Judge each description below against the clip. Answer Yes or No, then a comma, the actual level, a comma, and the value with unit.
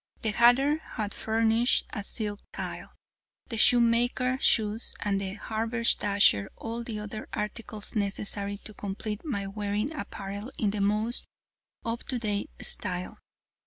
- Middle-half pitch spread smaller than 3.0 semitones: Yes, narrow, 2.4 semitones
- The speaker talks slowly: Yes, slow, 130 wpm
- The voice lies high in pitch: Yes, high, 215 Hz